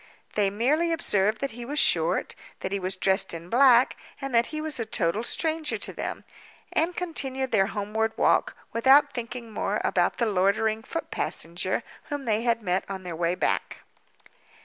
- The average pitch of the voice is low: No, high, 225 Hz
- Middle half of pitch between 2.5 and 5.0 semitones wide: No, wide, 5.6 semitones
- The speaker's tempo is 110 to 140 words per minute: No, average, 170 wpm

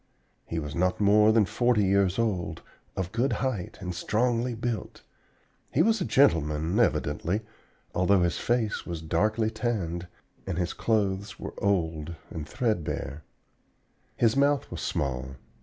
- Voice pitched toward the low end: Yes, low, 100 Hz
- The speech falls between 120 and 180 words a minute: Yes, average, 140 wpm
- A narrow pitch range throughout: No, wide, 5.4 semitones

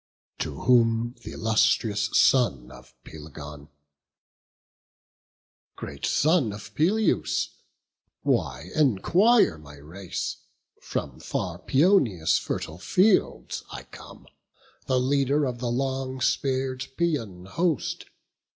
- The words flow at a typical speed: No, slow, 95 wpm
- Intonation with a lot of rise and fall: Yes, wide, 7.9 semitones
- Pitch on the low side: Yes, low, 120 Hz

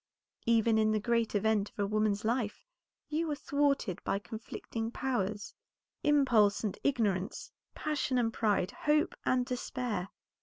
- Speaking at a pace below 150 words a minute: Yes, average, 140 wpm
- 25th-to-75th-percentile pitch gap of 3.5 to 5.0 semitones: Yes, average, 4.0 semitones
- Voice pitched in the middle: No, high, 225 Hz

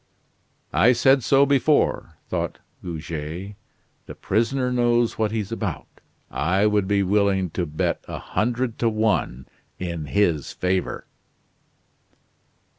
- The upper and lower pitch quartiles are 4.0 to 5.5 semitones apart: Yes, average, 4.6 semitones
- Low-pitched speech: Yes, low, 105 Hz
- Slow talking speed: Yes, slow, 115 wpm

